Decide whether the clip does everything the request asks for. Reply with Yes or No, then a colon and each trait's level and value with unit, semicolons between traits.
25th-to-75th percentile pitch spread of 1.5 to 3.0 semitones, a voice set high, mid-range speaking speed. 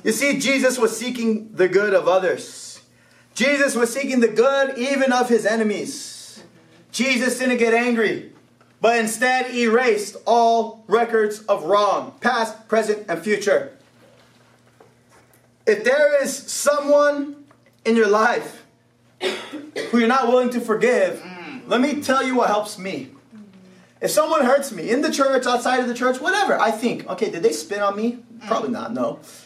No: average, 3.5 semitones; high, 240 Hz; average, 155 wpm